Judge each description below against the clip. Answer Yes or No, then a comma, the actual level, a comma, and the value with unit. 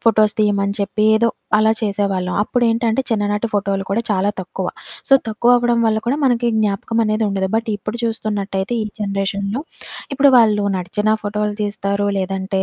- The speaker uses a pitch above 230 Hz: No, high, 210 Hz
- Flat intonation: Yes, narrow, 2.1 semitones